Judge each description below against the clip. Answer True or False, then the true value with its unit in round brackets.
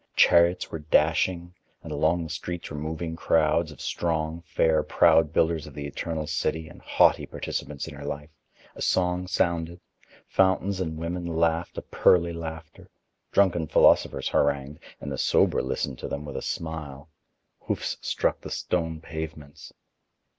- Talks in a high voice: False (80 Hz)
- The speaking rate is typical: True (155 wpm)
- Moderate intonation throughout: False (2.0 semitones)